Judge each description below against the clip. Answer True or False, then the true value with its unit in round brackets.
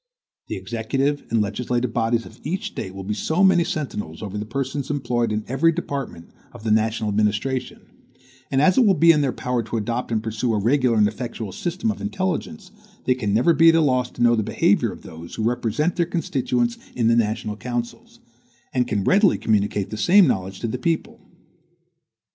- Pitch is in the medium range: False (120 Hz)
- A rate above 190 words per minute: True (200 wpm)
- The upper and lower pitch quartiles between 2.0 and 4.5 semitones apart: False (5.1 semitones)